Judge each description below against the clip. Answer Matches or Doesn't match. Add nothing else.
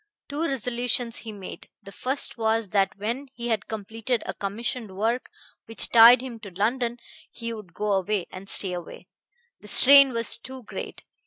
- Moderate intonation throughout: Matches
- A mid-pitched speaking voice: Doesn't match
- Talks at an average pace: Matches